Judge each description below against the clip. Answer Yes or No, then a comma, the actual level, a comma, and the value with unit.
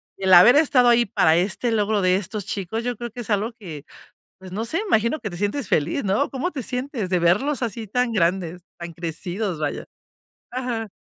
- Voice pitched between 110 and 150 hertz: No, high, 215 Hz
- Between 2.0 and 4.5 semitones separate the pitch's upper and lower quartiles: No, average, 4.9 semitones